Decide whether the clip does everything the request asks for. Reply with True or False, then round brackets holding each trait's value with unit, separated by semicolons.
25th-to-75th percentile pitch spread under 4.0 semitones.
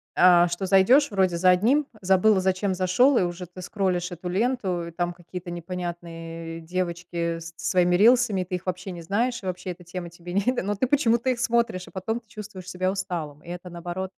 True (2.6 semitones)